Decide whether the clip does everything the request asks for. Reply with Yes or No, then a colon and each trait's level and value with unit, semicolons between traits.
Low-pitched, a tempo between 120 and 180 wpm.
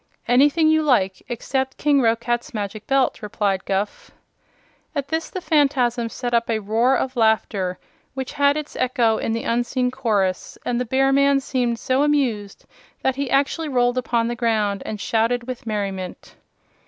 No: high, 245 Hz; average, 165 wpm